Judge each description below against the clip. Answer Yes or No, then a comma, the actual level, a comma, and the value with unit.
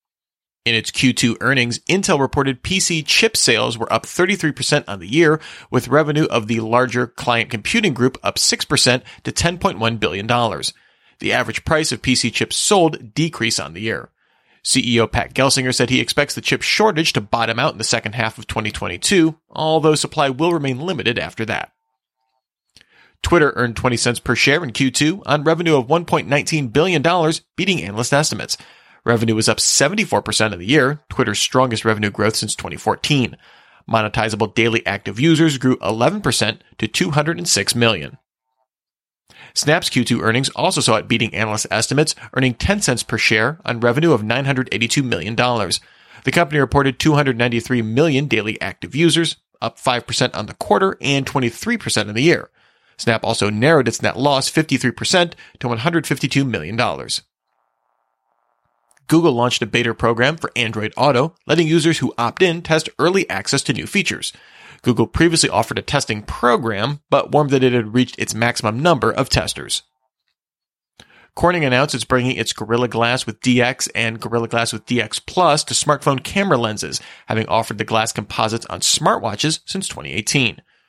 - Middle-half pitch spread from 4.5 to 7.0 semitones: Yes, average, 5.0 semitones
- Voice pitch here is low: Yes, low, 130 Hz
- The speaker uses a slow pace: No, average, 160 wpm